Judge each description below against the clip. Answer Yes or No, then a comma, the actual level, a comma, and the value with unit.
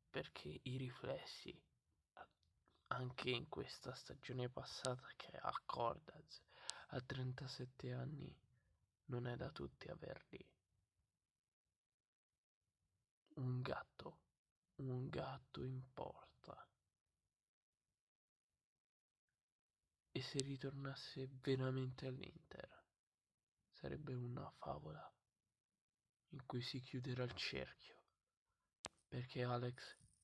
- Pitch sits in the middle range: No, low, 125 Hz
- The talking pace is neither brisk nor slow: No, slow, 80 wpm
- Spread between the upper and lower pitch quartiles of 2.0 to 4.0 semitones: No, average, 5.3 semitones